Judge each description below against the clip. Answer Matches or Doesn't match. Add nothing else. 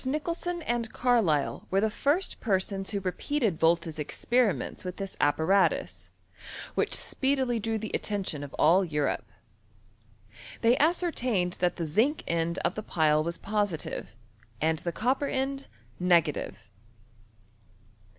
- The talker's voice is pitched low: Doesn't match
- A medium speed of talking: Doesn't match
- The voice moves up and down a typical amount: Doesn't match